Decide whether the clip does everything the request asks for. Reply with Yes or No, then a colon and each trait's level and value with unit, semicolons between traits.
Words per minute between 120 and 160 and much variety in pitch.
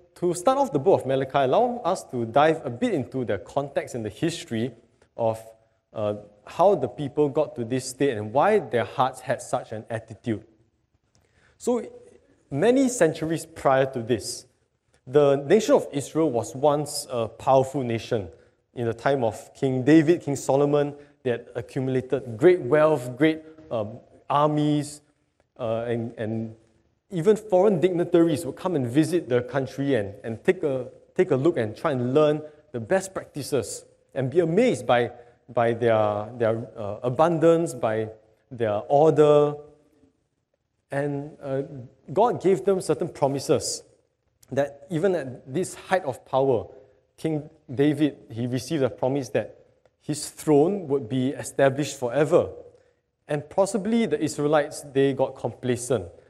No: average, 150 wpm; average, 4.7 semitones